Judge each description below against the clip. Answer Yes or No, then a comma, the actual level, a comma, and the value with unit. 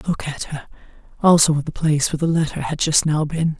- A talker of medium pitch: Yes, medium, 155 Hz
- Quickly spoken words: Yes, fast, 250 wpm